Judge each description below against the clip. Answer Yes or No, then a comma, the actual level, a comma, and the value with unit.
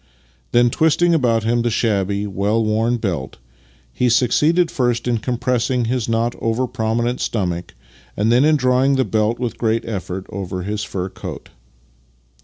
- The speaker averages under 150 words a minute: No, average, 160 wpm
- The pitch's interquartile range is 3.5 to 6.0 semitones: No, average, 2.8 semitones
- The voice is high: No, low, 115 Hz